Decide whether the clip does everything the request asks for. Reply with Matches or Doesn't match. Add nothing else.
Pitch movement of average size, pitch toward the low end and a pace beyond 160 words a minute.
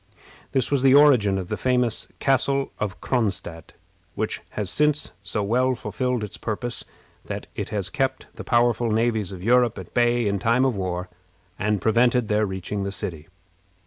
Matches